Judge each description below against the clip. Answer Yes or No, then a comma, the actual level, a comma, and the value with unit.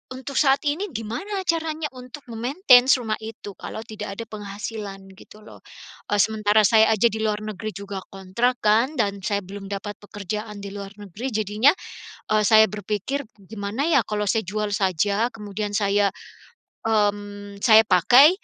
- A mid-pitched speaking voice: No, high, 215 Hz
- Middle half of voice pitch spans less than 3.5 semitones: Yes, narrow, 2.5 semitones